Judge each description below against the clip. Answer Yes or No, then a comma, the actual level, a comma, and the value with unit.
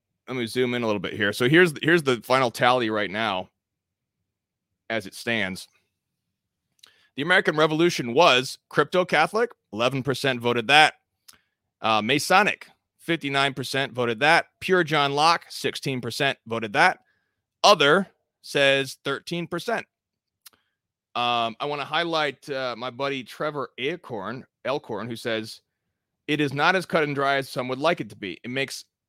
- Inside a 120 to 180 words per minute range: Yes, average, 155 wpm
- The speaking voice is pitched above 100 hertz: Yes, low, 135 Hz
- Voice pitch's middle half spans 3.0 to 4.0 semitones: No, average, 4.6 semitones